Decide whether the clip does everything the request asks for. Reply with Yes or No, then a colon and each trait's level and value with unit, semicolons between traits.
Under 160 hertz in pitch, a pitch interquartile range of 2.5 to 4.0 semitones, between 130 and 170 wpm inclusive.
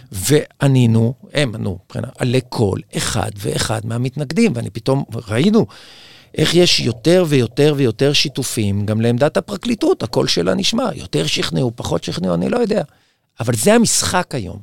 No: low, 135 Hz; average, 5.3 semitones; average, 145 wpm